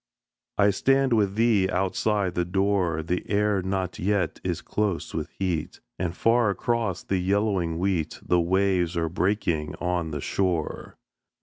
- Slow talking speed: No, average, 145 wpm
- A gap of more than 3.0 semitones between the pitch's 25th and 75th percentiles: No, average, 2.7 semitones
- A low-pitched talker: Yes, very low, 95 Hz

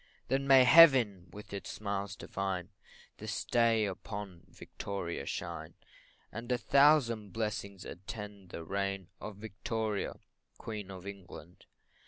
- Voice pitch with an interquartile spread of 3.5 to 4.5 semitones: No, average, 2.8 semitones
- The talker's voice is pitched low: Yes, low, 100 Hz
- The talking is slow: Yes, slow, 120 wpm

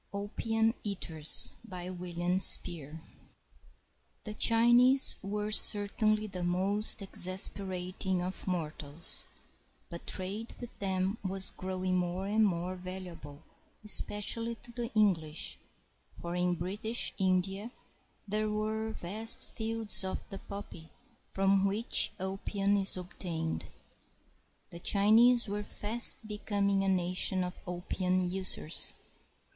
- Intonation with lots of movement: No, average, 2.8 semitones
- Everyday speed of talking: No, slow, 115 wpm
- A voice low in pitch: No, high, 195 Hz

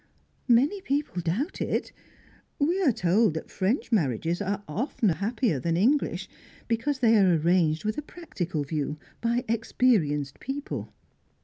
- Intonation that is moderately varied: No, wide, 7.3 semitones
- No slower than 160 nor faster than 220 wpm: No, slow, 135 wpm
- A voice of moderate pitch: No, high, 210 Hz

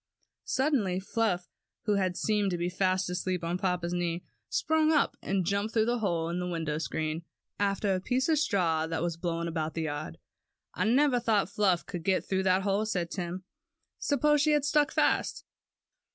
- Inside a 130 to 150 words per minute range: No, average, 185 wpm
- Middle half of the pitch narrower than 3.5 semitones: No, average, 4.1 semitones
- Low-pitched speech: No, medium, 185 Hz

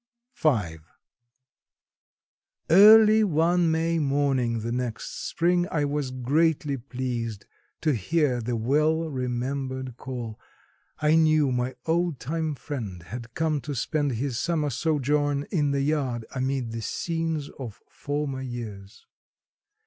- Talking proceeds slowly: Yes, slow, 120 wpm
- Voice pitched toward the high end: No, medium, 140 Hz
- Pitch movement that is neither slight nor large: Yes, average, 4.3 semitones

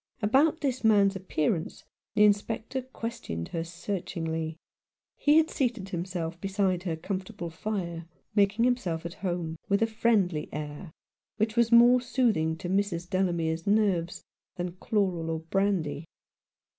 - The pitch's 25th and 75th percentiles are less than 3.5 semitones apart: No, average, 4.6 semitones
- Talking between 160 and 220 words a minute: No, slow, 135 wpm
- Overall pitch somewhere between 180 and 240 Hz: Yes, high, 190 Hz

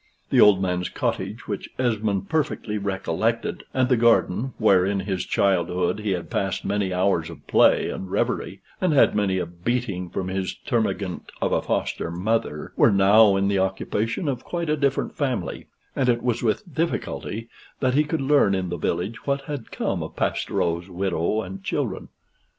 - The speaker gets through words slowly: No, average, 175 wpm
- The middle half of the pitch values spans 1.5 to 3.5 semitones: No, average, 4.7 semitones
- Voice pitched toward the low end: Yes, low, 100 Hz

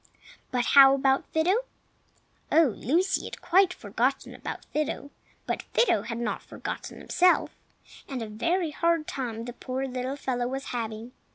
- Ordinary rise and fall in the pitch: Yes, average, 4.7 semitones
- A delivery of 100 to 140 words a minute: No, average, 150 wpm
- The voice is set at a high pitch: Yes, very high, 270 Hz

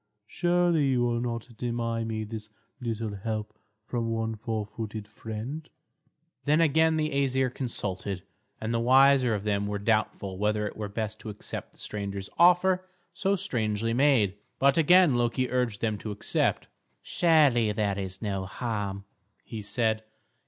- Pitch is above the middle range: No, low, 115 Hz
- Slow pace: No, average, 150 wpm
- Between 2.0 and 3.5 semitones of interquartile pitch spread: No, average, 4.1 semitones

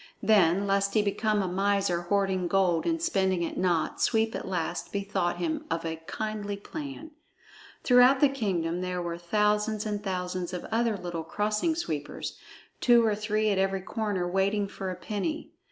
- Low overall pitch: No, high, 200 Hz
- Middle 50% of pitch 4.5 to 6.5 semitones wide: No, average, 3.2 semitones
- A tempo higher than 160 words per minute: Yes, average, 170 wpm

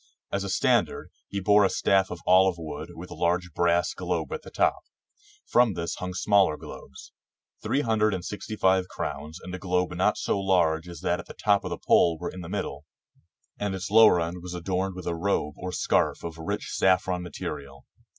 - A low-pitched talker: Yes, very low, 90 Hz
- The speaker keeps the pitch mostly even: Yes, narrow, 2.3 semitones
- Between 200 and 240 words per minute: Yes, fast, 205 wpm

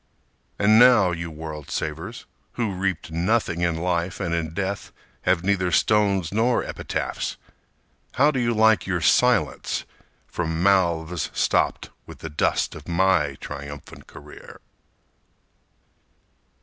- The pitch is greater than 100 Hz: No, very low, 90 Hz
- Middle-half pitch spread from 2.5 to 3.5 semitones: No, average, 4.2 semitones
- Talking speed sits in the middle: No, slow, 125 wpm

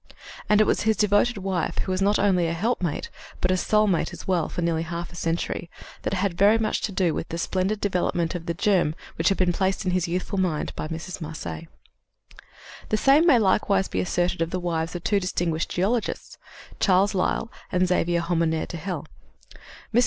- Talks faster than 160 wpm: Yes, average, 200 wpm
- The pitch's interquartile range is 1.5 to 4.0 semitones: Yes, average, 2.9 semitones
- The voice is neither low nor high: Yes, medium, 180 Hz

